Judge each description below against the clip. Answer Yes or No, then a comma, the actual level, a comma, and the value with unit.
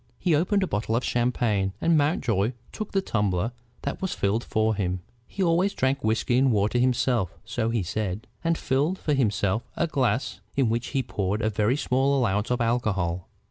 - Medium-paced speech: Yes, average, 185 wpm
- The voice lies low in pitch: Yes, low, 120 Hz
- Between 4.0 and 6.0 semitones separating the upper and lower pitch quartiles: Yes, average, 4.7 semitones